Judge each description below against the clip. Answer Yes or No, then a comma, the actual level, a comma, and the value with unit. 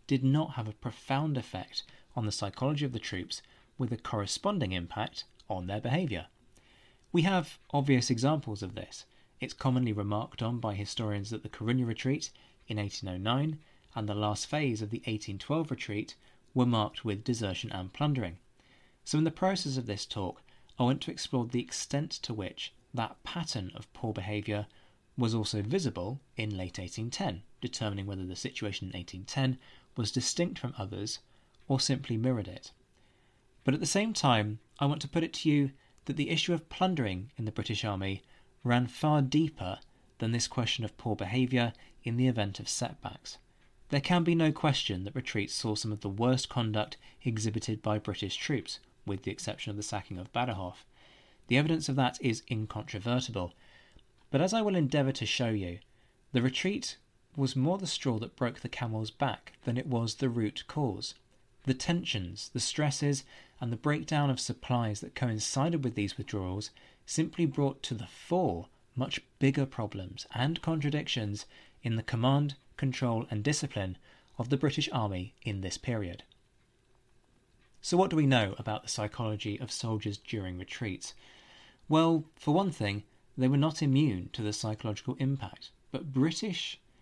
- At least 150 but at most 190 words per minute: Yes, average, 170 wpm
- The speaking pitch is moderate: No, low, 120 Hz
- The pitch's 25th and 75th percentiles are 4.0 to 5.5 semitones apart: Yes, average, 4.5 semitones